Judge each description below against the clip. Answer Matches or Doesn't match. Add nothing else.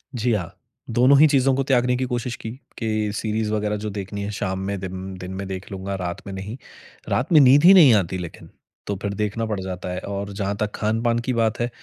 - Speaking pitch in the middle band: Doesn't match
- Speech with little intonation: Doesn't match